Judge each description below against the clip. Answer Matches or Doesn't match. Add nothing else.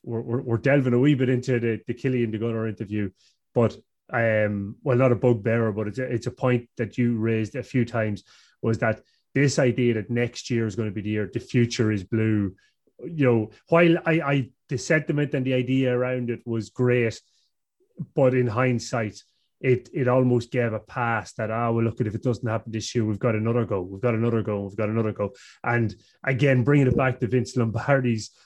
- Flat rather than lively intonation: Matches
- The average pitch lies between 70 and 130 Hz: Matches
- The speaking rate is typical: Doesn't match